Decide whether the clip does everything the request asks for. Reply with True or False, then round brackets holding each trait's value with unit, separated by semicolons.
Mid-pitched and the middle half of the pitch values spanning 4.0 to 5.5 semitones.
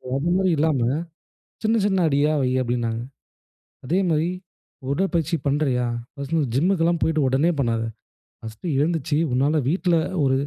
True (150 Hz; 4.4 semitones)